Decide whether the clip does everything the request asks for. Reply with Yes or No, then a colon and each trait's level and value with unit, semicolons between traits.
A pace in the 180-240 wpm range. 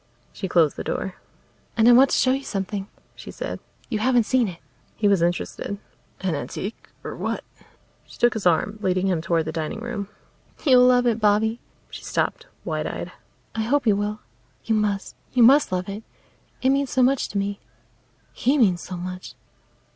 Yes: average, 185 wpm